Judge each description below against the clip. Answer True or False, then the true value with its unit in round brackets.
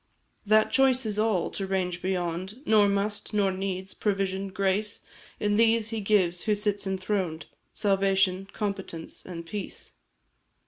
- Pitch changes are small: True (2.0 semitones)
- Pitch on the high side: True (195 Hz)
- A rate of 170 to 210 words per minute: False (135 wpm)